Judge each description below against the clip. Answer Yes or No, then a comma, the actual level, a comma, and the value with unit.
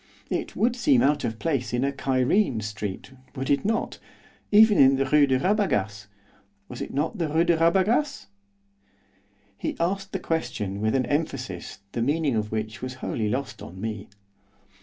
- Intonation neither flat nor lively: No, wide, 7.6 semitones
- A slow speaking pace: No, average, 170 wpm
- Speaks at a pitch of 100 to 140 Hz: Yes, low, 135 Hz